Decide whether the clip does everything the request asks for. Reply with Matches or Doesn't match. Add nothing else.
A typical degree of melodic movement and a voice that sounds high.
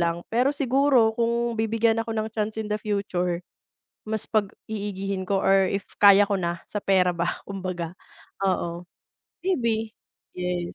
Matches